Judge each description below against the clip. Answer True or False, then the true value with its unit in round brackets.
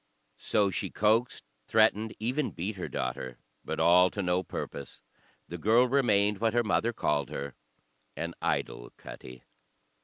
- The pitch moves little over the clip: False (4.9 semitones)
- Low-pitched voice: True (100 Hz)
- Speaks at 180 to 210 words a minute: False (145 wpm)